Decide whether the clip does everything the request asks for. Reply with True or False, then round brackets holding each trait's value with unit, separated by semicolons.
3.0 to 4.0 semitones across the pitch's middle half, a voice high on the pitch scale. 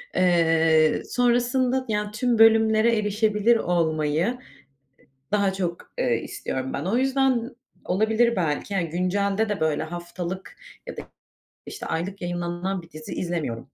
False (4.7 semitones; 195 Hz)